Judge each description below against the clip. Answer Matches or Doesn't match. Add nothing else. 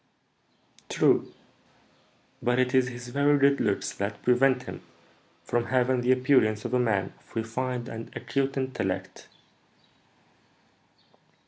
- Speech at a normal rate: Doesn't match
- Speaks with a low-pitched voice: Matches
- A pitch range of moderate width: Doesn't match